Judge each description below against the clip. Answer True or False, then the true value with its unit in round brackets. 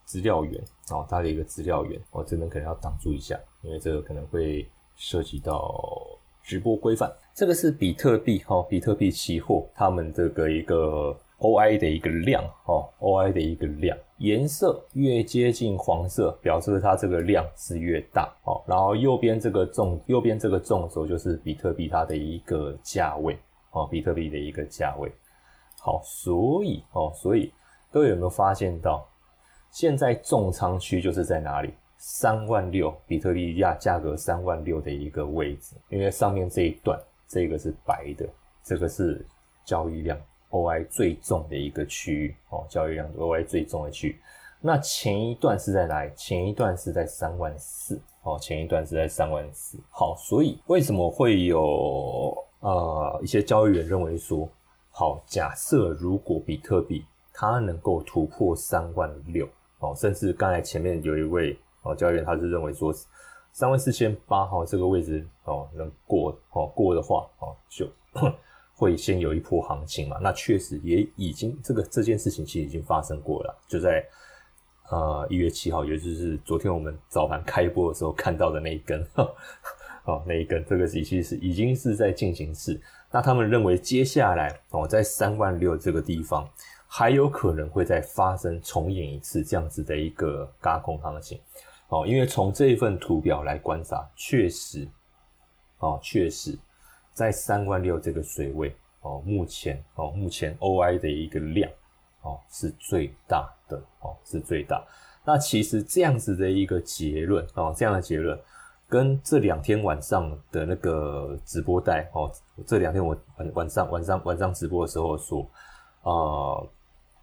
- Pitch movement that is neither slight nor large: True (5.0 semitones)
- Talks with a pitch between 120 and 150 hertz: False (90 Hz)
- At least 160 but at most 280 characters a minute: True (255 characters per minute)